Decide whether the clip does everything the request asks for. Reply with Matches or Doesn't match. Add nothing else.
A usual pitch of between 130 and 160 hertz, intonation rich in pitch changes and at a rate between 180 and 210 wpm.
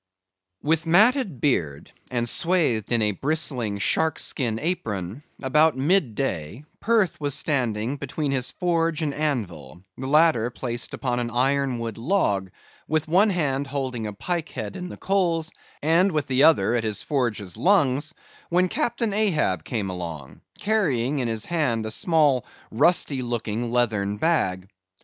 Doesn't match